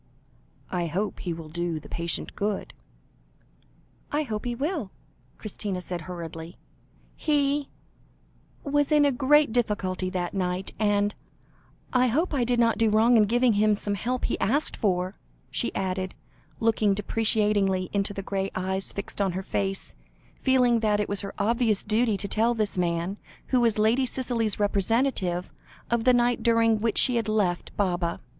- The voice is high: Yes, high, 210 Hz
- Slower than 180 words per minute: Yes, average, 160 wpm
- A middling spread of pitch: Yes, average, 4.0 semitones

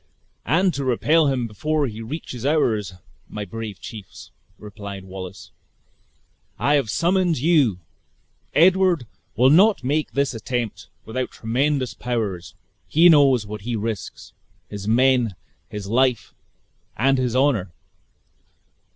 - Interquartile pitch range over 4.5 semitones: Yes, wide, 5.4 semitones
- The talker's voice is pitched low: Yes, low, 125 Hz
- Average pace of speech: No, slow, 120 wpm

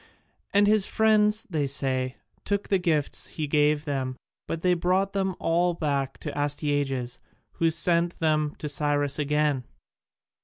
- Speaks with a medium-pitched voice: Yes, medium, 150 Hz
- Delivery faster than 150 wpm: No, average, 145 wpm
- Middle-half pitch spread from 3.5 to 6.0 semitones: Yes, average, 3.8 semitones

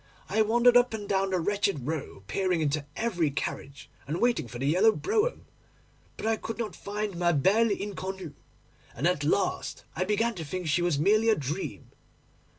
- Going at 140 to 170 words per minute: No, average, 180 wpm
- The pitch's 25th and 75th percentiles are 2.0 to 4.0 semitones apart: No, wide, 5.5 semitones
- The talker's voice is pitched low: No, high, 190 Hz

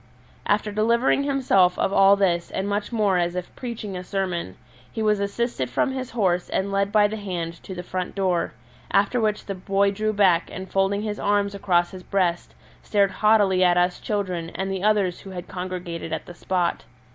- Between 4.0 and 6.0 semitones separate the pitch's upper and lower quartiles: No, narrow, 2.5 semitones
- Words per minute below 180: No, average, 195 wpm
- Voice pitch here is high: Yes, high, 195 Hz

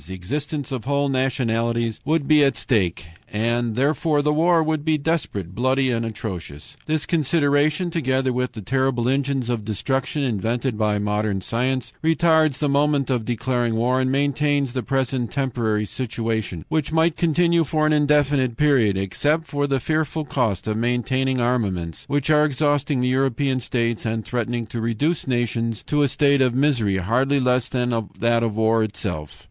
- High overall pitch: No, low, 130 Hz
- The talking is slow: No, average, 165 wpm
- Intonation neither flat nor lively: Yes, average, 4.0 semitones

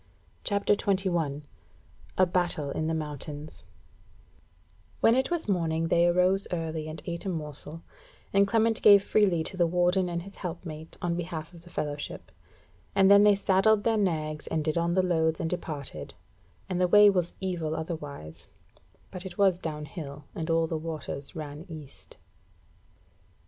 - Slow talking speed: No, average, 160 wpm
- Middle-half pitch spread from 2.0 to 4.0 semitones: Yes, average, 3.3 semitones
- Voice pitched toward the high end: No, medium, 170 Hz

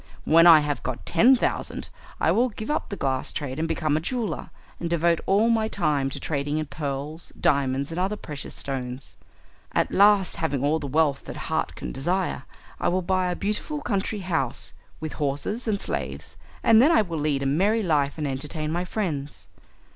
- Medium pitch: Yes, medium, 160 Hz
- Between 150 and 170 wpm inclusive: No, average, 190 wpm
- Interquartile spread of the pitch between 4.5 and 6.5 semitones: Yes, wide, 5.6 semitones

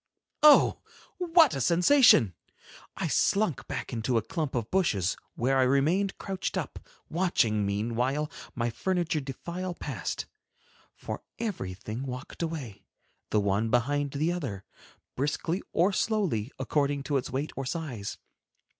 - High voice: No, medium, 140 Hz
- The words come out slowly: Yes, slow, 130 wpm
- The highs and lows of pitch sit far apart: Yes, wide, 7.0 semitones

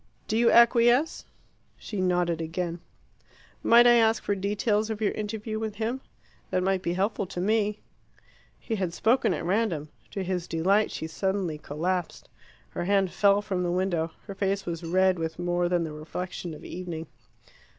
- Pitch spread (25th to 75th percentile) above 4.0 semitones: No, average, 3.5 semitones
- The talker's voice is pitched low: No, high, 190 Hz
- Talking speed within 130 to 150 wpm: No, average, 170 wpm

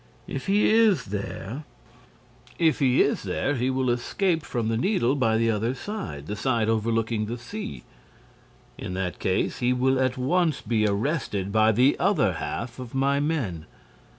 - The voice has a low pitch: Yes, low, 120 Hz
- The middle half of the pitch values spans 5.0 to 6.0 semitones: No, average, 4.5 semitones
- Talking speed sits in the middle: Yes, average, 165 wpm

